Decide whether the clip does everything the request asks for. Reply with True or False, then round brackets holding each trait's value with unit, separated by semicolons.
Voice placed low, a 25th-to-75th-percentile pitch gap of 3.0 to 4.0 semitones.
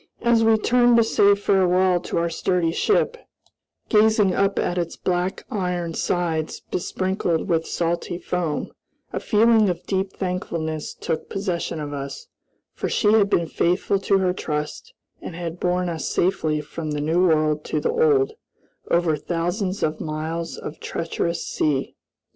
False (175 Hz; 3.4 semitones)